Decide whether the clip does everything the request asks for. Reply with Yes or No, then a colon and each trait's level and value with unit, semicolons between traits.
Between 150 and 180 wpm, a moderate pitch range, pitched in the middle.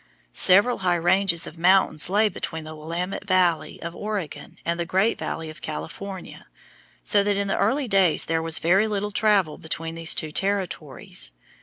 Yes: average, 170 wpm; average, 3.4 semitones; medium, 180 Hz